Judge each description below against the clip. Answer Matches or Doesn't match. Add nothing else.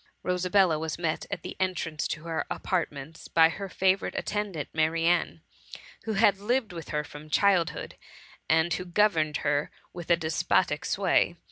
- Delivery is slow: Doesn't match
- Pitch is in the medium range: Matches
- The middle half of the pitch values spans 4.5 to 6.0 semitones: Doesn't match